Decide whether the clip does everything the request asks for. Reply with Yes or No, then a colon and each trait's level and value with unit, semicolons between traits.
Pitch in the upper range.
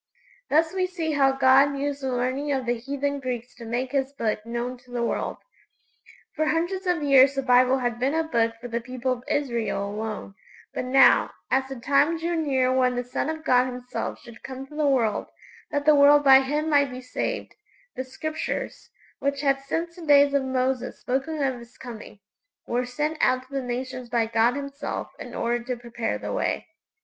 Yes: very high, 265 Hz